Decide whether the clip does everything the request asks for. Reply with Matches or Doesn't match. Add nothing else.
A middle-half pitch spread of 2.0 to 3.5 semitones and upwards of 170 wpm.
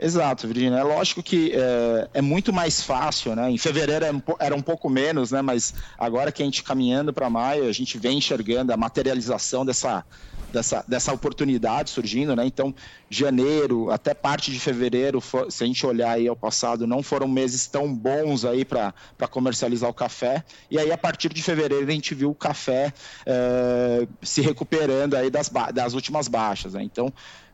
Matches